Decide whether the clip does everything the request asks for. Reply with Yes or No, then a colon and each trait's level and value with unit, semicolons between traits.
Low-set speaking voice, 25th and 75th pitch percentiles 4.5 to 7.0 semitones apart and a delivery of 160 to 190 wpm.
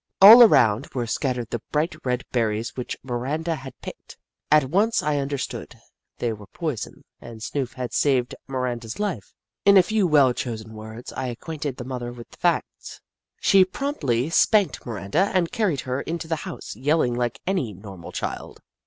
Yes: low, 130 Hz; wide, 5.4 semitones; average, 170 wpm